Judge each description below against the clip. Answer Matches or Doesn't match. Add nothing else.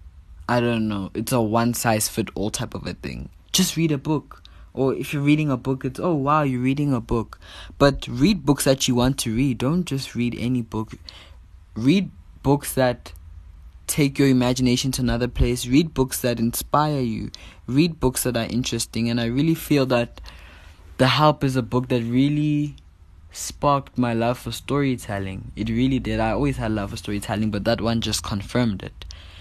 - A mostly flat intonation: Doesn't match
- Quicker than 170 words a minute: Matches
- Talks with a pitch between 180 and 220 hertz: Doesn't match